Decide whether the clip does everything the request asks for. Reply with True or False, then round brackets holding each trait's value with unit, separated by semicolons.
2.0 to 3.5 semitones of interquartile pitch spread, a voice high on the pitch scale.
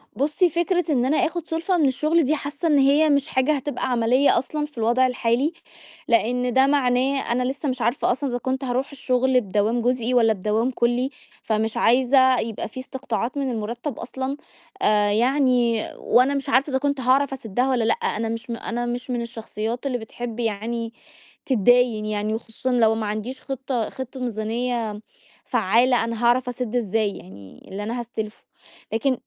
True (2.9 semitones; 245 Hz)